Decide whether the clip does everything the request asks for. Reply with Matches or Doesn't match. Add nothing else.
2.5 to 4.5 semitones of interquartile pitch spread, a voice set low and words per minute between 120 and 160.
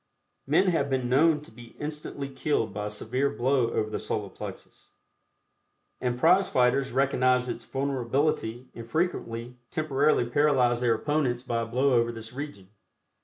Matches